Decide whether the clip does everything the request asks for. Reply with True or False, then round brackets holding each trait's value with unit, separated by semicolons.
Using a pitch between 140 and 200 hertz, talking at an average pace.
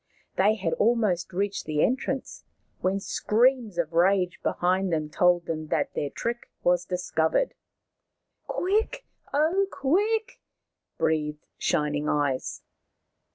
False (185 Hz; 120 wpm)